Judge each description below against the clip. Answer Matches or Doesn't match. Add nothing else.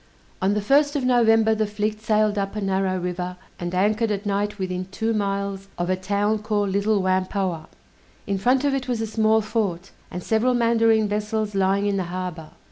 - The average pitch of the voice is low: Doesn't match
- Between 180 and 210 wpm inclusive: Matches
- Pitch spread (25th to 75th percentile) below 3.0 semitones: Matches